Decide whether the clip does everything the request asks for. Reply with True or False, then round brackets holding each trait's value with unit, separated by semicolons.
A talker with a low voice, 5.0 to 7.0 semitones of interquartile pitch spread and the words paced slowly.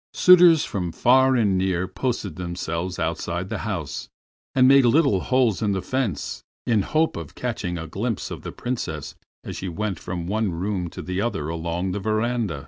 False (100 Hz; 5.5 semitones; 185 wpm)